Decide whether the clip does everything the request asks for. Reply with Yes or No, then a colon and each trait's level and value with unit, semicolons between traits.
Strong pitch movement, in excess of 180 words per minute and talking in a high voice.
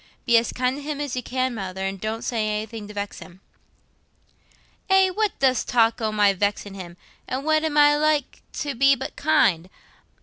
Yes: wide, 5.9 semitones; average, 195 wpm; high, 240 Hz